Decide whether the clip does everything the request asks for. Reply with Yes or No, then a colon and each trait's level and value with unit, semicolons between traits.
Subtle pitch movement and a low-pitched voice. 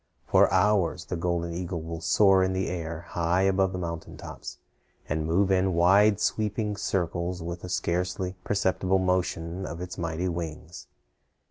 Yes: narrow, 2.0 semitones; very low, 90 Hz